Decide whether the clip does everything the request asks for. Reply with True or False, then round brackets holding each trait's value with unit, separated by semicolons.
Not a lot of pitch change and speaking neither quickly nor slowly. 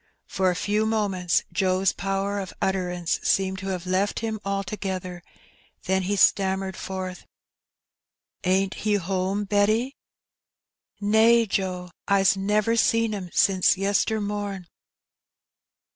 False (1.7 semitones; 125 wpm)